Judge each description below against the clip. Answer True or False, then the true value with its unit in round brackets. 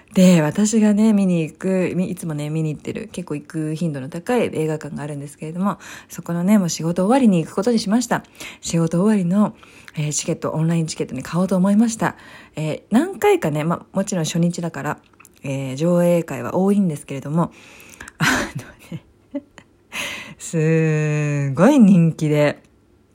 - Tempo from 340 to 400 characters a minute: True (345 characters per minute)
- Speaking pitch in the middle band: True (170 Hz)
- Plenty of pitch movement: False (4.3 semitones)